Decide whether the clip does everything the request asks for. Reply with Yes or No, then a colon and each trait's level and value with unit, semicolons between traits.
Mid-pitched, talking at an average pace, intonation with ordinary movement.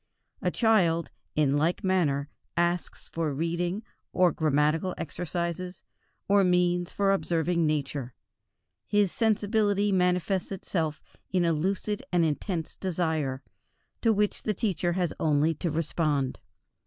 No: medium, 175 Hz; slow, 120 wpm; average, 3.3 semitones